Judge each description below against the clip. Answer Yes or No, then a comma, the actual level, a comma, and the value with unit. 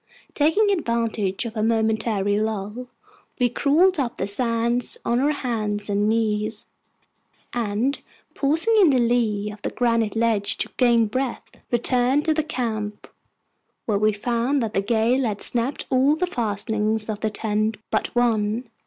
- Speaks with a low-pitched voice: No, high, 230 Hz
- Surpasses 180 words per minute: No, average, 155 wpm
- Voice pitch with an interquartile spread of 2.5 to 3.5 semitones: Yes, average, 3.0 semitones